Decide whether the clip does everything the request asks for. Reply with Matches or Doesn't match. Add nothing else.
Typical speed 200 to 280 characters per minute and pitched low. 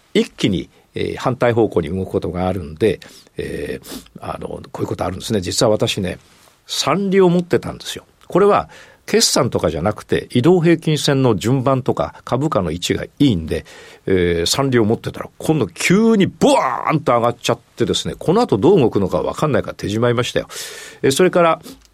Doesn't match